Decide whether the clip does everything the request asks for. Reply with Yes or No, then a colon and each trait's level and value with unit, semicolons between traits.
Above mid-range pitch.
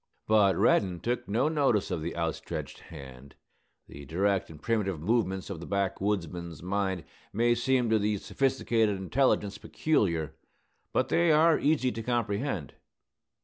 No: low, 100 Hz